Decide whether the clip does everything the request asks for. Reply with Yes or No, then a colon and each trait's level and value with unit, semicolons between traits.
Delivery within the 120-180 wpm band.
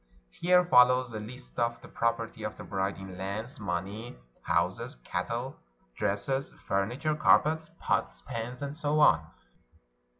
Yes: average, 140 wpm